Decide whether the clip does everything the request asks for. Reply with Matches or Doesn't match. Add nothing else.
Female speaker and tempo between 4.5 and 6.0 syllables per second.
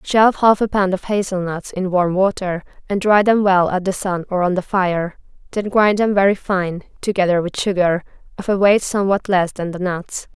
Matches